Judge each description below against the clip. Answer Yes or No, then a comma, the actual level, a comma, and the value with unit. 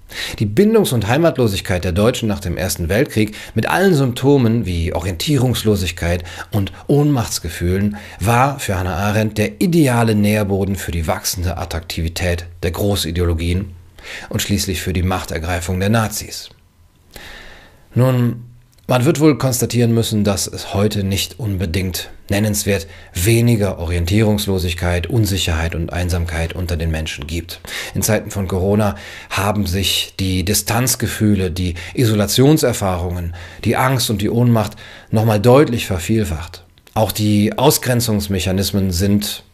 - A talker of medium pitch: No, low, 100 Hz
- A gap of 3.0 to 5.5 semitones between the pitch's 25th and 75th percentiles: Yes, average, 3.7 semitones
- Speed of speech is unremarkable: No, slow, 120 wpm